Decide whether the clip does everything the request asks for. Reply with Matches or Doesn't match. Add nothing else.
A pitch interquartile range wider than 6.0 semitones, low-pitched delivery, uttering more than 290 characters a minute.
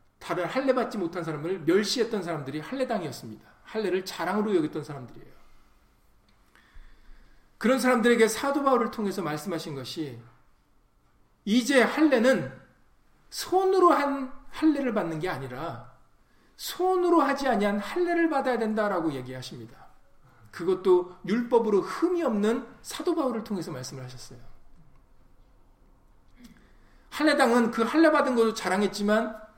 Doesn't match